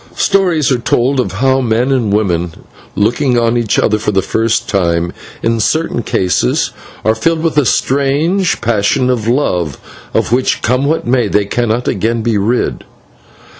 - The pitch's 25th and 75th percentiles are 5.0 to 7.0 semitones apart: No, average, 4.3 semitones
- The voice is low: Yes, low, 120 Hz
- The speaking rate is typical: Yes, average, 170 wpm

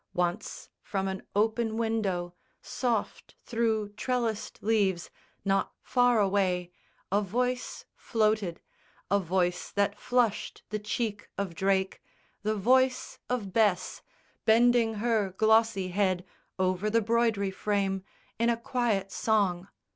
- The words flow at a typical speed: No, slow, 115 wpm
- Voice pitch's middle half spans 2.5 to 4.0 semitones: Yes, average, 3.0 semitones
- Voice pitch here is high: Yes, high, 210 Hz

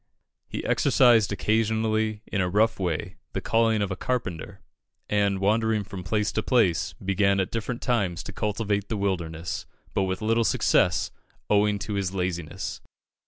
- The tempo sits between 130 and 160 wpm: Yes, average, 155 wpm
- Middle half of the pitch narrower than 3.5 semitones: Yes, average, 2.8 semitones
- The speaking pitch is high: No, low, 100 Hz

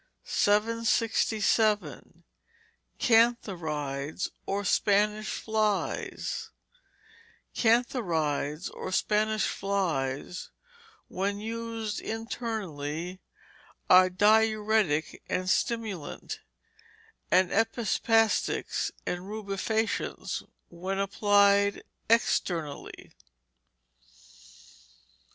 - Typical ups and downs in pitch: Yes, average, 3.4 semitones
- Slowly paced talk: Yes, slow, 55 wpm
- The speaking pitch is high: Yes, high, 205 Hz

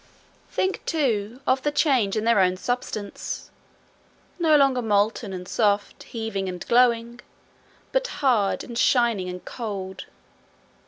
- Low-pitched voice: No, high, 230 Hz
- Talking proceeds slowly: Yes, slow, 125 wpm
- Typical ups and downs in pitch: Yes, average, 4.1 semitones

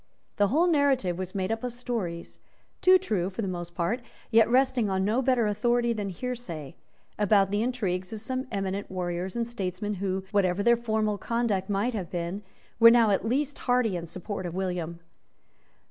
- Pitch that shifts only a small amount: No, average, 4.3 semitones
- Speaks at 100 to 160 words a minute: No, average, 180 wpm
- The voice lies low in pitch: No, high, 205 Hz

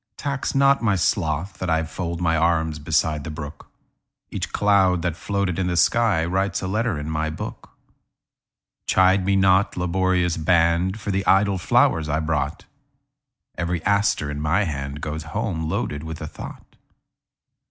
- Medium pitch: No, very low, 85 Hz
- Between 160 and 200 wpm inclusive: No, slow, 135 wpm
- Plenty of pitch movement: No, average, 3.4 semitones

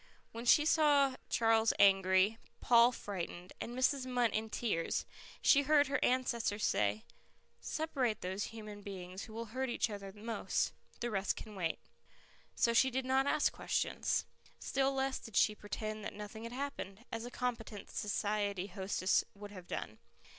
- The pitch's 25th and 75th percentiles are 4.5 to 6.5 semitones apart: No, average, 4.0 semitones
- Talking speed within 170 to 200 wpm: No, average, 160 wpm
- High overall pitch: Yes, high, 225 Hz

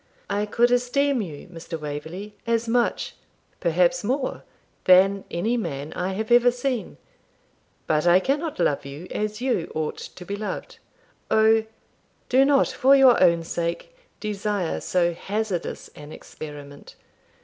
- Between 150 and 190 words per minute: No, average, 140 wpm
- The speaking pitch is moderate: No, high, 205 Hz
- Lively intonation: Yes, wide, 6.2 semitones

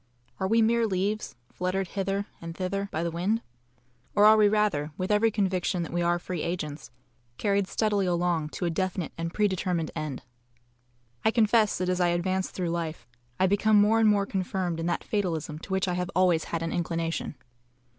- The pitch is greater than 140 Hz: Yes, medium, 185 Hz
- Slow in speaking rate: No, average, 195 wpm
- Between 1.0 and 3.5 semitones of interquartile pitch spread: Yes, average, 3.1 semitones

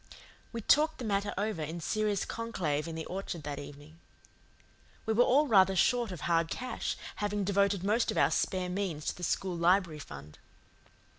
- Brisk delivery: No, average, 175 wpm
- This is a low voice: No, high, 190 Hz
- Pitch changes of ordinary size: Yes, average, 4.7 semitones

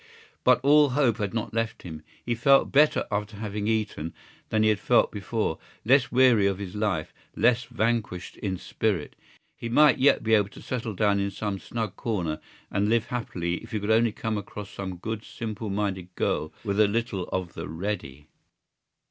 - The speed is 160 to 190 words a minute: Yes, average, 185 wpm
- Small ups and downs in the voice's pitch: No, average, 3.0 semitones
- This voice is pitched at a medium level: No, low, 105 Hz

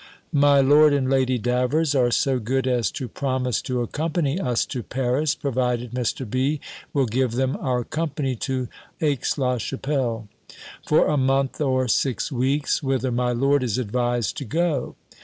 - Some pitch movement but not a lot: No, narrow, 2.2 semitones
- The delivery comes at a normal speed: Yes, average, 160 wpm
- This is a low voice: Yes, low, 130 Hz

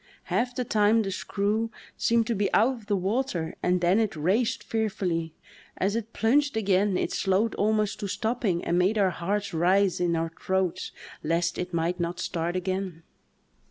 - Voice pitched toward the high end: Yes, high, 195 Hz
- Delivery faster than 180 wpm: No, average, 170 wpm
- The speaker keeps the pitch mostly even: No, average, 3.7 semitones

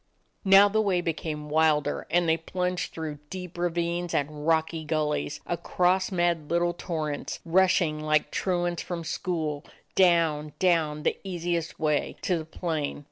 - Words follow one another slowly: No, average, 145 wpm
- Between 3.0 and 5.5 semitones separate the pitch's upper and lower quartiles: No, narrow, 2.5 semitones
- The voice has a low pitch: No, medium, 165 Hz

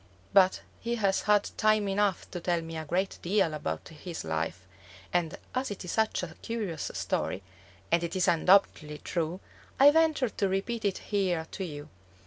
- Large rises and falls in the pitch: No, average, 4.2 semitones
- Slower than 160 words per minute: No, average, 170 wpm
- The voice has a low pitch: No, medium, 185 Hz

